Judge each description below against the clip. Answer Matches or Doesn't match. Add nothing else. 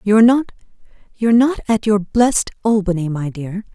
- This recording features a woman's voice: Matches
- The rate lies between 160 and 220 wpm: Doesn't match